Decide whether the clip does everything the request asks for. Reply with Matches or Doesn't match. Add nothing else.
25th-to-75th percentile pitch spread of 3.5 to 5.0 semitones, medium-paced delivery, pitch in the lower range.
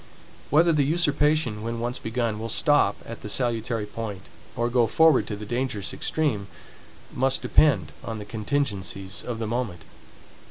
Matches